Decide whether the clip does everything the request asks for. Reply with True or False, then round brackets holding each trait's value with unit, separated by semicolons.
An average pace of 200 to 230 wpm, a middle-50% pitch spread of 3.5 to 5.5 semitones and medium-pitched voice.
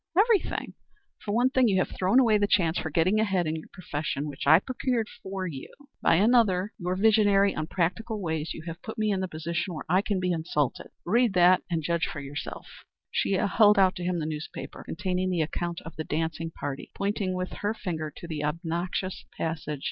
True (205 wpm; 4.0 semitones; 180 Hz)